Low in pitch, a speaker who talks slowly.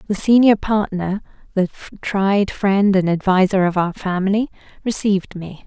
No: high, 195 Hz; slow, 115 wpm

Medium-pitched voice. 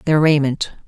Yes: medium, 150 Hz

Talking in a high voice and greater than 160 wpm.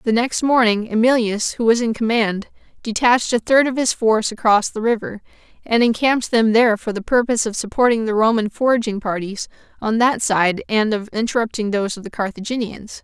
Yes: high, 225 Hz; average, 185 wpm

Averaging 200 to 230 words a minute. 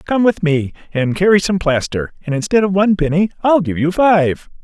Yes: fast, 205 wpm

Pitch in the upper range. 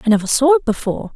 Yes: very high, 250 Hz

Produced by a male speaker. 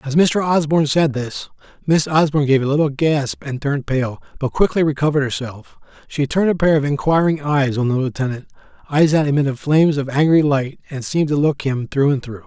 Yes: male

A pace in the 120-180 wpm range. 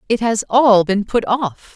No: fast, 205 wpm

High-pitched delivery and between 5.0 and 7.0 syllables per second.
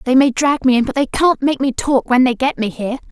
Yes: very high, 260 Hz; 6.0 syllables/s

